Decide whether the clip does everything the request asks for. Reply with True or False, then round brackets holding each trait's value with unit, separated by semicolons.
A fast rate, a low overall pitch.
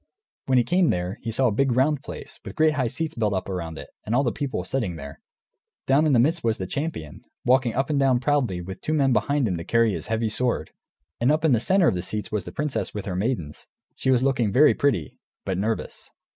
True (245 wpm; 120 Hz)